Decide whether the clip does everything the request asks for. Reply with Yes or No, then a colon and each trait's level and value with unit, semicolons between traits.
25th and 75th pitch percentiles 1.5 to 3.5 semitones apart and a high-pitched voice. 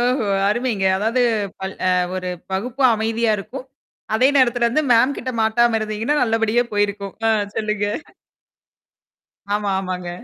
Yes: average, 2.8 semitones; high, 225 Hz